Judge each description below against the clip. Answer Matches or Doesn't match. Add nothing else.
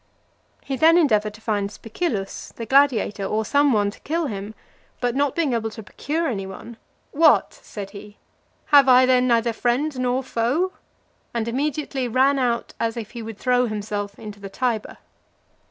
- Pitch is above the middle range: Matches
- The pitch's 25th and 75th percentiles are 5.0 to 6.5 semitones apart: Doesn't match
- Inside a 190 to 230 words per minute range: Doesn't match